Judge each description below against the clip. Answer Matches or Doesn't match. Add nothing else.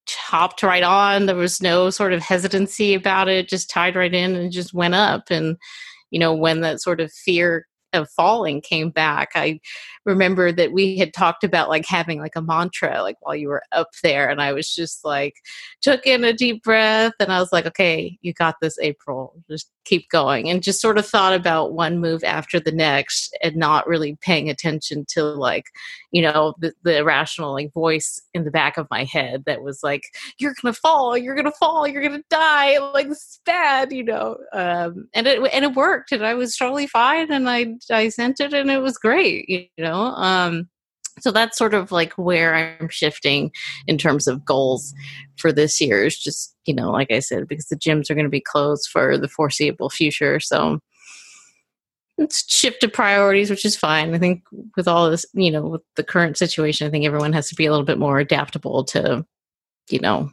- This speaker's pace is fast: Matches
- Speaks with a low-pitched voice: Doesn't match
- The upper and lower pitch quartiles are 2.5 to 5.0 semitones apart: Doesn't match